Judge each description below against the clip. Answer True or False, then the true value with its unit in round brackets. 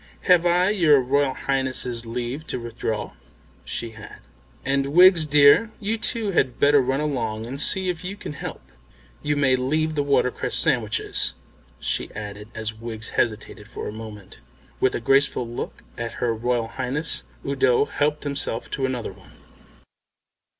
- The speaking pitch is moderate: False (130 Hz)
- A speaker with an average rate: True (155 wpm)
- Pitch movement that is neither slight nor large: True (4.4 semitones)